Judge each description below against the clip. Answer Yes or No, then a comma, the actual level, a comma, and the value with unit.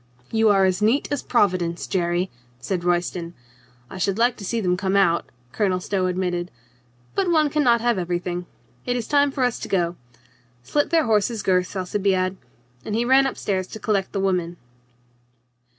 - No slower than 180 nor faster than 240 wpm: Yes, average, 185 wpm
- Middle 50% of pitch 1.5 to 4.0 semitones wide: No, average, 4.5 semitones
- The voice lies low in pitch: No, high, 195 Hz